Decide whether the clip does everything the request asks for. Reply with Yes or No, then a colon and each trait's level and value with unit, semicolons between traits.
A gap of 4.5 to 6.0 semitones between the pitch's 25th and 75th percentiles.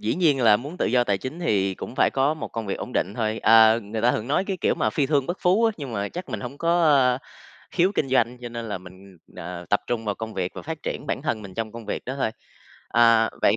Yes: average, 5.2 semitones